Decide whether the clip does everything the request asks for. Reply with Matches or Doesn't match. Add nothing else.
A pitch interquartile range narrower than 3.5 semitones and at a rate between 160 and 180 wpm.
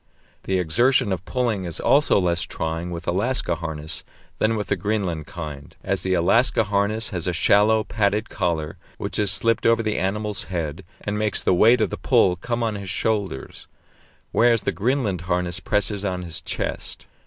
Doesn't match